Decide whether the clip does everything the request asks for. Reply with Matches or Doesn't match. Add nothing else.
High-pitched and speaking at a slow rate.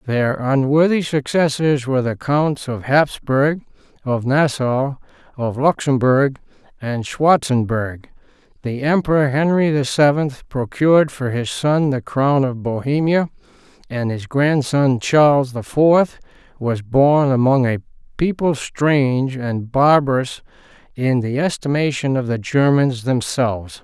Doesn't match